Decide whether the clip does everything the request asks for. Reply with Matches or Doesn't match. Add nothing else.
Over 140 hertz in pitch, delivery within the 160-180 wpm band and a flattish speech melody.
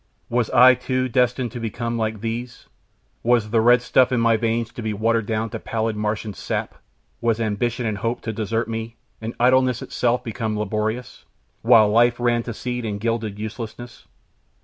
Doesn't match